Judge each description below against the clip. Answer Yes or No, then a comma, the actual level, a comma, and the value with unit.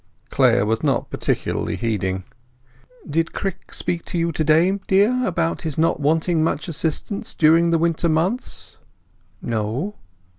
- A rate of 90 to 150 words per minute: Yes, average, 140 wpm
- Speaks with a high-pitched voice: No, medium, 165 Hz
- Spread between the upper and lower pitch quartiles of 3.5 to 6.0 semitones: No, average, 2.7 semitones